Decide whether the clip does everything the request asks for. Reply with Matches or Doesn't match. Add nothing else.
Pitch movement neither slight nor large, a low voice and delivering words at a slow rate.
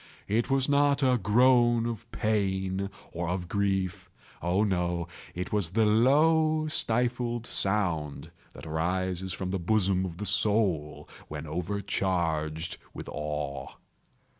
Matches